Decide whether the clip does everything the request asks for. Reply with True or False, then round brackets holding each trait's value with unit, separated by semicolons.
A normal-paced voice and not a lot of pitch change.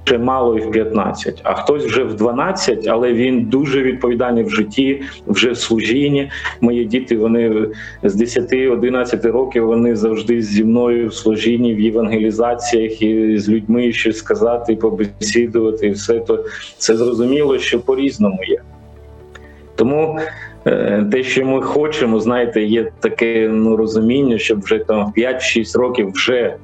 True (145 wpm; 2.2 semitones)